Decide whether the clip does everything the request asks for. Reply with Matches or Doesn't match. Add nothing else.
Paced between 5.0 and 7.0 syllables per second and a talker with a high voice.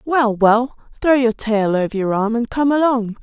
Doesn't match